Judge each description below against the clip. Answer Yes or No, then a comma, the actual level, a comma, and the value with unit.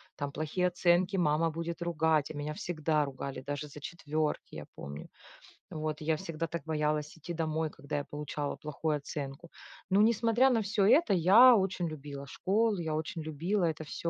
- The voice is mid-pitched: Yes, medium, 160 Hz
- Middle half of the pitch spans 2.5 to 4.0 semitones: Yes, average, 3.2 semitones